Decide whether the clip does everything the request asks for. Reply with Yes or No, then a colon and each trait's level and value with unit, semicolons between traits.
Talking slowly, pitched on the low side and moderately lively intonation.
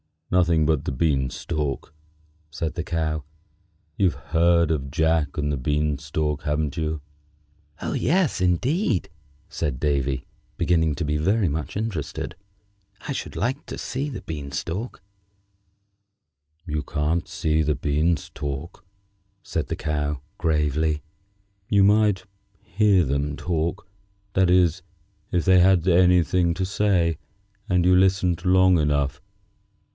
Yes: slow, 130 wpm; very low, 80 Hz; average, 3.5 semitones